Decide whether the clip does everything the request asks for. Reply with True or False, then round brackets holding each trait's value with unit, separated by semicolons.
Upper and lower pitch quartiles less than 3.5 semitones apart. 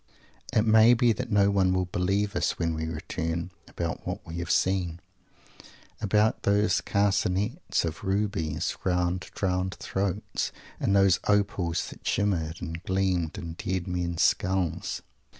True (2.9 semitones)